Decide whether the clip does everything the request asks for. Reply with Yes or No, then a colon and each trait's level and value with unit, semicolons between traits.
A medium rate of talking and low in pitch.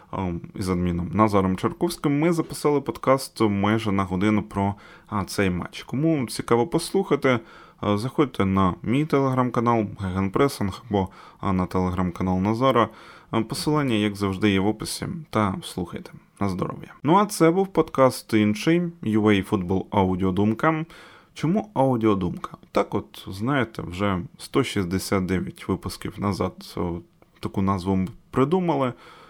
Yes: average, 115 wpm; low, 110 Hz